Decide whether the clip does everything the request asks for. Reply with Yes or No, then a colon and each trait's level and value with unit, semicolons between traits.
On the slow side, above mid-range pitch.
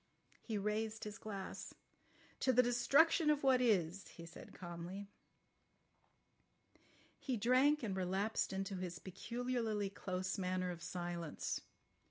Yes: slow, 120 wpm; high, 200 Hz